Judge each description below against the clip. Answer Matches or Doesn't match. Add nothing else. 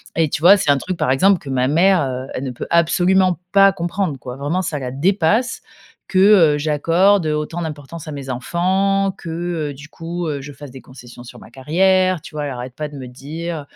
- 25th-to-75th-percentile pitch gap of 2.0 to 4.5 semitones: Doesn't match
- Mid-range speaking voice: Matches